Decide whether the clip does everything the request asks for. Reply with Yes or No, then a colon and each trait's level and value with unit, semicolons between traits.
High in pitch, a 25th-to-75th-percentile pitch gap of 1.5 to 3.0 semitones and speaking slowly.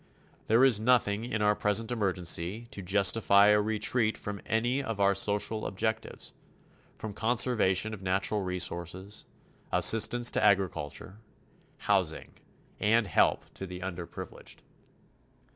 No: low, 105 Hz; average, 2.7 semitones; slow, 120 wpm